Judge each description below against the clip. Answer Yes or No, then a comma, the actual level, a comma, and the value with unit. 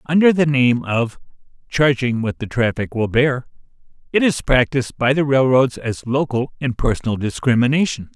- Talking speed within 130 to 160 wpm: Yes, average, 155 wpm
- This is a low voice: Yes, low, 130 Hz